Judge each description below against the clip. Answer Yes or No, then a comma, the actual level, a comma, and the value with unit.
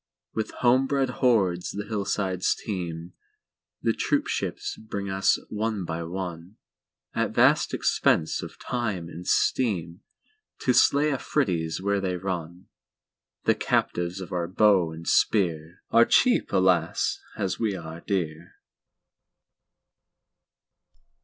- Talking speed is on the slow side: Yes, slow, 100 wpm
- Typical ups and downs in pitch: Yes, average, 4.0 semitones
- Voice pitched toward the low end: Yes, very low, 95 Hz